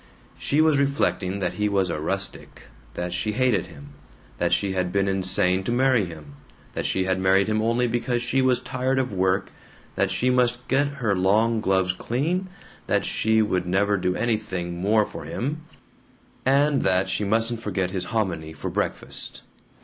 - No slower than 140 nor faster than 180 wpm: Yes, average, 175 wpm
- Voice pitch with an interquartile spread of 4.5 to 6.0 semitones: Yes, average, 4.8 semitones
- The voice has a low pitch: Yes, low, 105 Hz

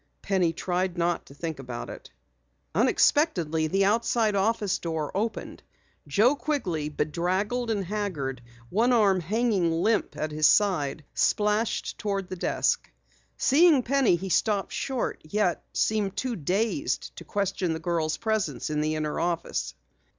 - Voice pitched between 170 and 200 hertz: Yes, high, 190 Hz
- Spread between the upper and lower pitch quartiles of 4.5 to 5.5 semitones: Yes, average, 5.2 semitones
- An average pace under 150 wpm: Yes, average, 140 wpm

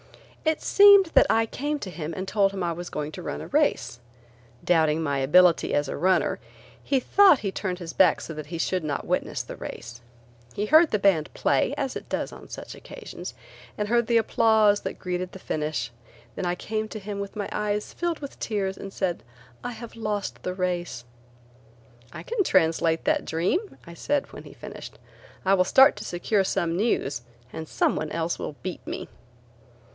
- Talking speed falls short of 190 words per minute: No, average, 195 wpm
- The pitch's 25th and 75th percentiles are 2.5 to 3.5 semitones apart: No, average, 5.2 semitones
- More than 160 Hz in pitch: Yes, high, 190 Hz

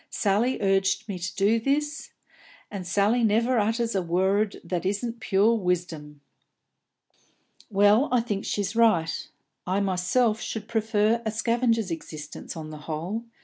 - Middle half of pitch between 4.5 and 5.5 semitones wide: No, average, 3.8 semitones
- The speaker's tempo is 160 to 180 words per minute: No, average, 140 wpm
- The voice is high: Yes, high, 205 Hz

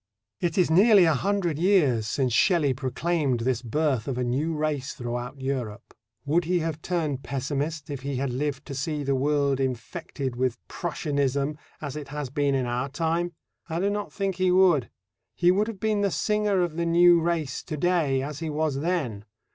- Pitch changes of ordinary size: Yes, average, 4.5 semitones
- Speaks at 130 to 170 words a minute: No, average, 190 wpm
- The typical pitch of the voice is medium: Yes, medium, 150 Hz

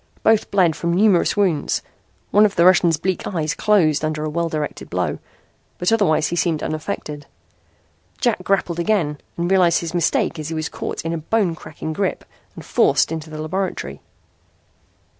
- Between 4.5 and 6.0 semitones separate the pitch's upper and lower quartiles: No, average, 3.5 semitones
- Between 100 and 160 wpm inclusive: No, average, 170 wpm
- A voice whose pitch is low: No, medium, 170 Hz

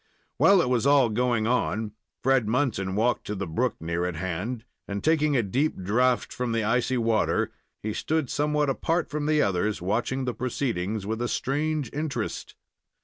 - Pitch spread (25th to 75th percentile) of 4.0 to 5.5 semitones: Yes, average, 4.9 semitones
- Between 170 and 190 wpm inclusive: Yes, average, 175 wpm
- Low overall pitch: Yes, low, 120 Hz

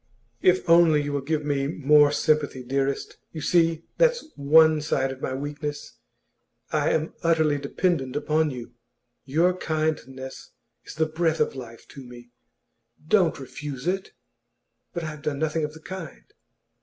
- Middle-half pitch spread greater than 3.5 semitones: No, narrow, 2.6 semitones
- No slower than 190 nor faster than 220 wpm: No, average, 155 wpm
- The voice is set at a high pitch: No, medium, 150 Hz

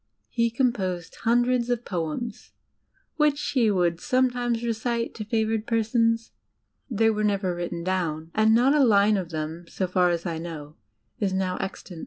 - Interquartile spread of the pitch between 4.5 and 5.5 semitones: Yes, average, 5.0 semitones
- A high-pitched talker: Yes, high, 215 Hz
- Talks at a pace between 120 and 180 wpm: Yes, average, 160 wpm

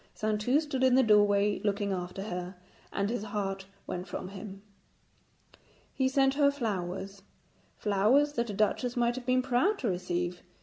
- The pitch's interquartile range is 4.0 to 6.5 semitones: Yes, average, 4.7 semitones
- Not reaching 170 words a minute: Yes, average, 160 wpm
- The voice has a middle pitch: No, high, 210 Hz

